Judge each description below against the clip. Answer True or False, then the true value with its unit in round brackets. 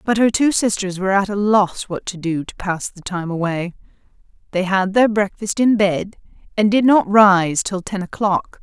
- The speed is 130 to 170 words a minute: False (200 wpm)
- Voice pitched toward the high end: True (195 Hz)